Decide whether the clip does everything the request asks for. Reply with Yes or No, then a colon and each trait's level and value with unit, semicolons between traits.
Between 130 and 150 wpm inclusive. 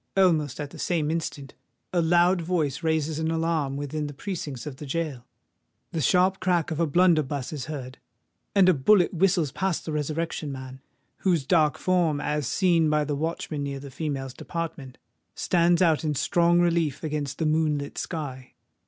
No: average, 170 wpm